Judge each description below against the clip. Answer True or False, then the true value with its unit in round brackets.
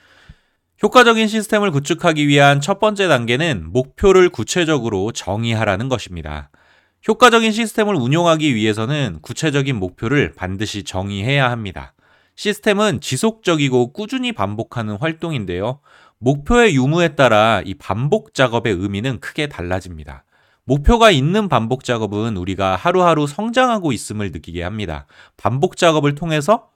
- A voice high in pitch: False (135 Hz)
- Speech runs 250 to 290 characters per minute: False (345 characters per minute)